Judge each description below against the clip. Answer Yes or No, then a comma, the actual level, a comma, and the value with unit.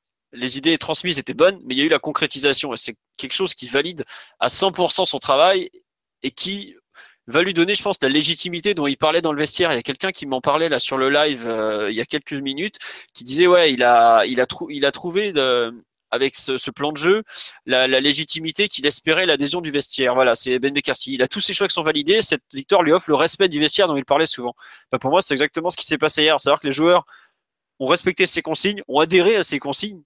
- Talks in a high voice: No, medium, 150 Hz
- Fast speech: Yes, fast, 255 wpm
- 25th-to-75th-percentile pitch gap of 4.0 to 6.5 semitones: Yes, average, 5.0 semitones